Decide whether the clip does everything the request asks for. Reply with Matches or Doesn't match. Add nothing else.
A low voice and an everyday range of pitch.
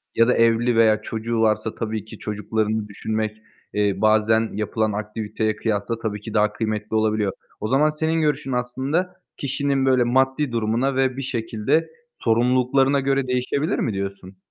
Matches